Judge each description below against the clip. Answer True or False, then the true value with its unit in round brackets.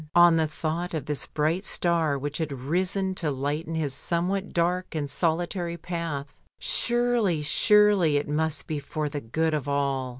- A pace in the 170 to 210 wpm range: True (175 wpm)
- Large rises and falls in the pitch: False (3.2 semitones)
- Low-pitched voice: False (160 Hz)